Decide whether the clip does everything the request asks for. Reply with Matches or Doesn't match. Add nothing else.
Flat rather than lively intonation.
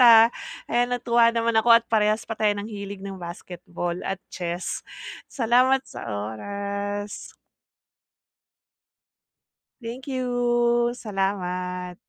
Doesn't match